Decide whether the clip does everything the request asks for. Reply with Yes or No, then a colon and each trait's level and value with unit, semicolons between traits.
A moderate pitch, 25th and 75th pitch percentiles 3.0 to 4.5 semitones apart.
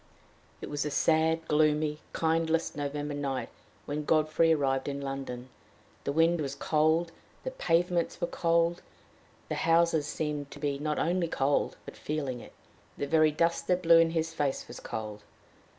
No: medium, 155 Hz; narrow, 2.5 semitones